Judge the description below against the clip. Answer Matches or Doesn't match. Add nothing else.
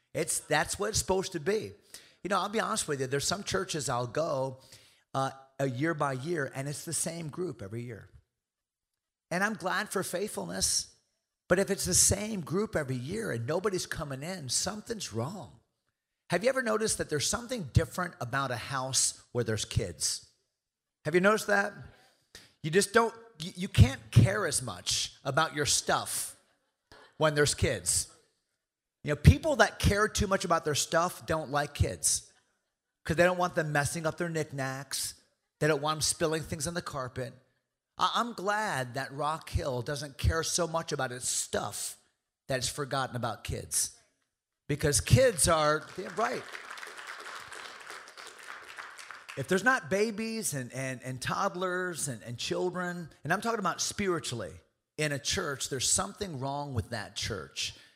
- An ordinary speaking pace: Matches